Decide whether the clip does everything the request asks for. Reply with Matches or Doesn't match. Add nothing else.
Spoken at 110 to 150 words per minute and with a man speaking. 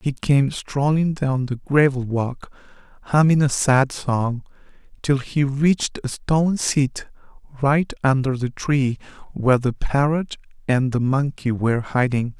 Matches